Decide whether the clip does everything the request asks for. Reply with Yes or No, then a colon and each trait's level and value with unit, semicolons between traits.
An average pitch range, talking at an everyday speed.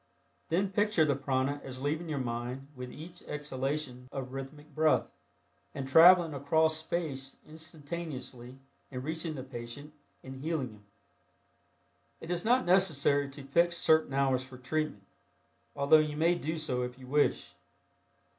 Yes: average, 3.3 semitones; average, 145 wpm